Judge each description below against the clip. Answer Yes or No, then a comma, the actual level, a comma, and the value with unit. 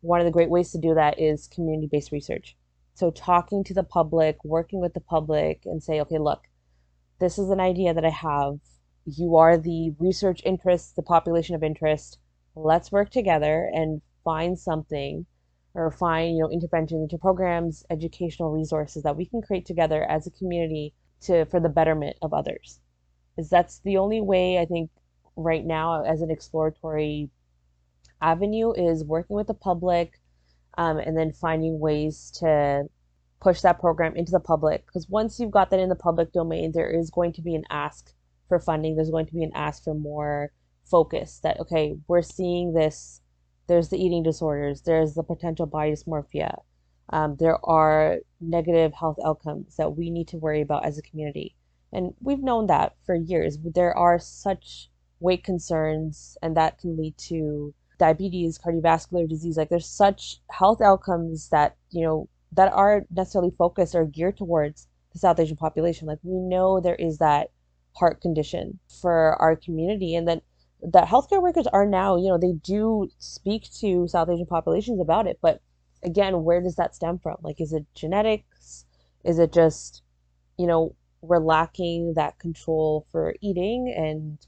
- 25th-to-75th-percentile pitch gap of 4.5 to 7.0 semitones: No, narrow, 2.6 semitones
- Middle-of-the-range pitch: Yes, medium, 165 Hz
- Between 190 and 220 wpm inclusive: No, average, 175 wpm